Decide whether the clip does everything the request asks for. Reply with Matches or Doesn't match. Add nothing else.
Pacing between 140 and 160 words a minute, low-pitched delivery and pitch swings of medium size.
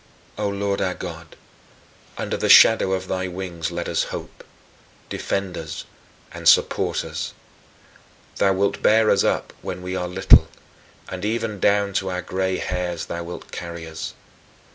Doesn't match